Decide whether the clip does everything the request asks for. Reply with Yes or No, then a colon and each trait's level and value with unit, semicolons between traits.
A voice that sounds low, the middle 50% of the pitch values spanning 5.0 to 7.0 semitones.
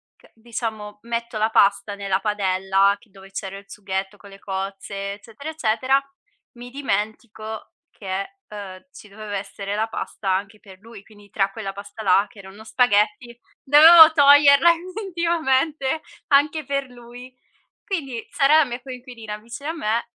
No: high, 220 Hz; wide, 5.4 semitones